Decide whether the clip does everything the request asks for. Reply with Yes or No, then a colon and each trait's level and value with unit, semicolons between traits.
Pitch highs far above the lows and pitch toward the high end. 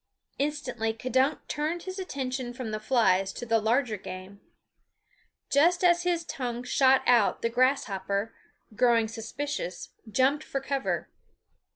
No: average, 4.3 semitones; very high, 250 Hz